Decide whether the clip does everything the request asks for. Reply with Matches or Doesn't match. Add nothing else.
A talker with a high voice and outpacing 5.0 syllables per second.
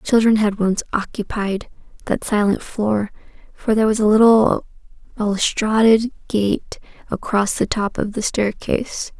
Doesn't match